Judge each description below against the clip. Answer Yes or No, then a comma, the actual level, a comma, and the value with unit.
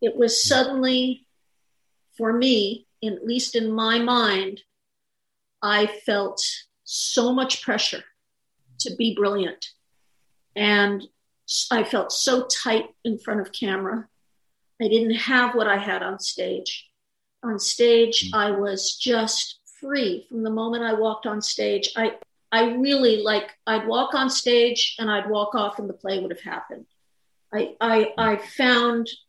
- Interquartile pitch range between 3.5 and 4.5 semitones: No, narrow, 2.5 semitones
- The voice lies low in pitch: No, high, 225 Hz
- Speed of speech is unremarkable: Yes, average, 145 wpm